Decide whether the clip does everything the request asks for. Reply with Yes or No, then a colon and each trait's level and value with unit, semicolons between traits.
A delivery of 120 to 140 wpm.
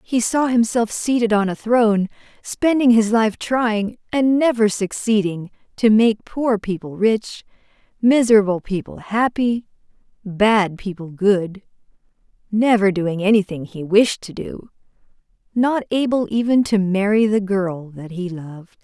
Yes: slow, 135 wpm